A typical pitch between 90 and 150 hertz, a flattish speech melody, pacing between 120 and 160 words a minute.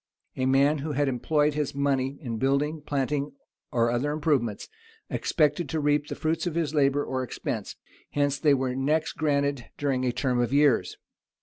No: medium, 140 Hz; narrow, 2.1 semitones; average, 175 wpm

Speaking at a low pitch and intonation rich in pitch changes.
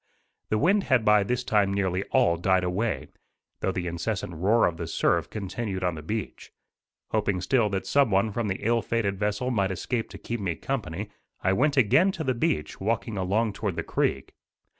No: low, 105 Hz; average, 3.8 semitones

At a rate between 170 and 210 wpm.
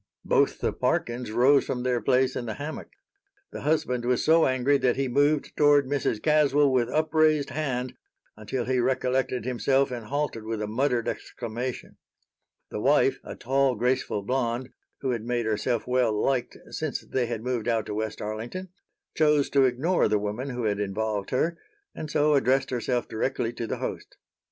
Yes: average, 175 wpm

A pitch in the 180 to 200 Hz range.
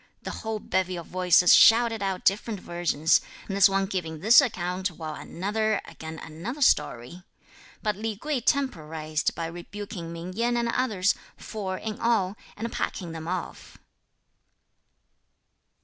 Yes: high, 190 Hz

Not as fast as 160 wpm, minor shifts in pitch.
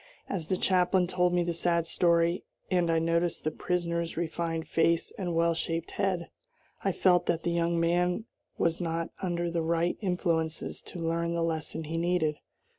No: average, 175 wpm; narrow, 1.1 semitones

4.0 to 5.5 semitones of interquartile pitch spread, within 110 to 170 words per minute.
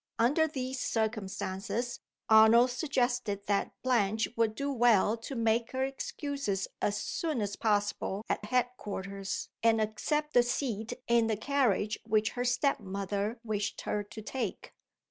No: average, 3.3 semitones; average, 145 wpm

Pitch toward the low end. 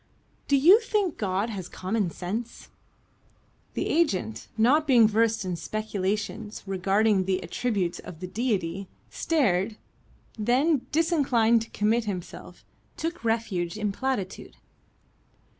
No: high, 215 Hz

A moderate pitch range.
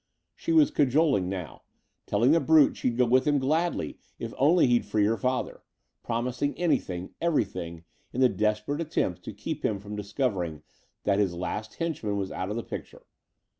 No: wide, 6.3 semitones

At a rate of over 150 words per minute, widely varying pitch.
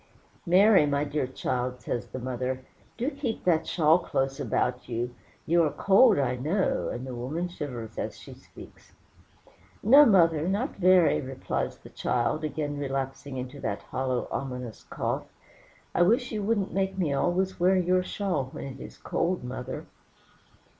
Yes: average, 160 wpm; wide, 6.3 semitones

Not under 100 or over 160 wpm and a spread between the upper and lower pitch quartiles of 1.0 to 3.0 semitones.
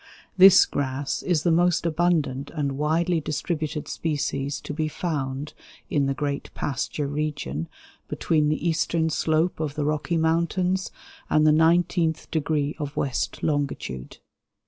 Yes: slow, 135 wpm; narrow, 2.5 semitones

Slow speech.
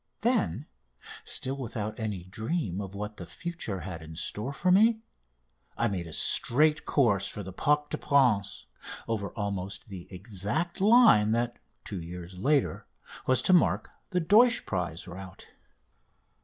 No: average, 145 wpm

